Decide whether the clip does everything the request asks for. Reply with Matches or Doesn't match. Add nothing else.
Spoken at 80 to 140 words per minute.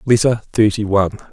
Matches